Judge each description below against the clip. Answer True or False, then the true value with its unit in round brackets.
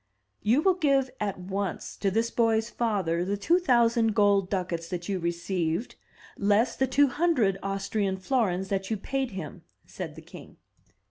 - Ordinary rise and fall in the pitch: True (4.1 semitones)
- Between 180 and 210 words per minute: False (160 wpm)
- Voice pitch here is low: False (205 Hz)